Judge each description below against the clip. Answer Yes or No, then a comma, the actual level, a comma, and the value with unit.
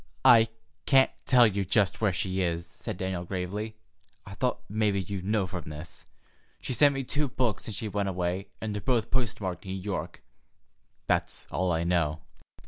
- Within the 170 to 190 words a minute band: Yes, average, 180 wpm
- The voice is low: Yes, low, 100 Hz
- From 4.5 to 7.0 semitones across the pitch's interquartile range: No, average, 3.6 semitones